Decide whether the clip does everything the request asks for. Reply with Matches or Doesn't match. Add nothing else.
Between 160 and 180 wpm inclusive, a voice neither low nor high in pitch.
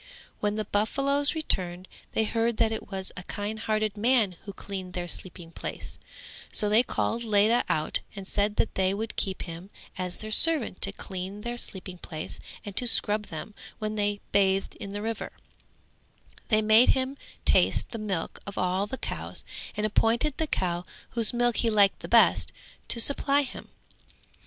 Doesn't match